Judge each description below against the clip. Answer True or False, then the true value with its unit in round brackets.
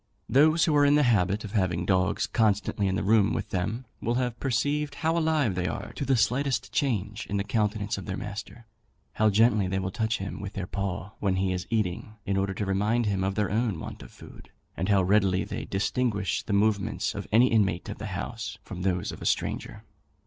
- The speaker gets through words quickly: True (220 wpm)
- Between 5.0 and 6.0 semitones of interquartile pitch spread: False (3.6 semitones)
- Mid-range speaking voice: False (105 Hz)